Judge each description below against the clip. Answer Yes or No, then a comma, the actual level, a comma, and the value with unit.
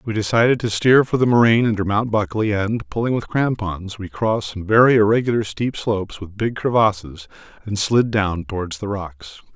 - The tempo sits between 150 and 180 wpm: No, average, 190 wpm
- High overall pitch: No, low, 105 Hz